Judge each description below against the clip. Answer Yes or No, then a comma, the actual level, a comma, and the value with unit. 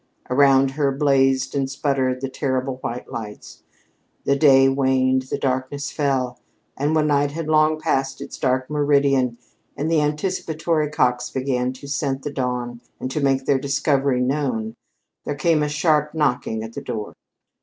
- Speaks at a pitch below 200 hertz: Yes, low, 135 Hz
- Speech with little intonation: Yes, narrow, 2.3 semitones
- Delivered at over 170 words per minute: No, average, 160 wpm